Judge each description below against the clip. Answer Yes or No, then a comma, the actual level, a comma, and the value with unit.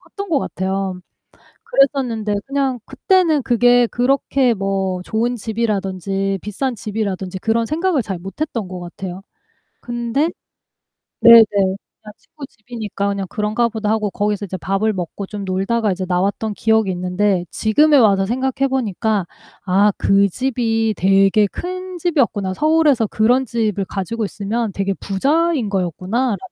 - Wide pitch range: No, average, 4.0 semitones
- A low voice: No, high, 215 Hz